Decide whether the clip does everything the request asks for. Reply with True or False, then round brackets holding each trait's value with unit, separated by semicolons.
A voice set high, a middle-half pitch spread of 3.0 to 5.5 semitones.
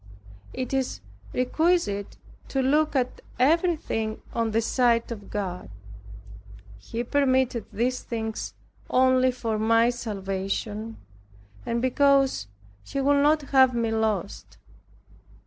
True (240 Hz; 3.4 semitones)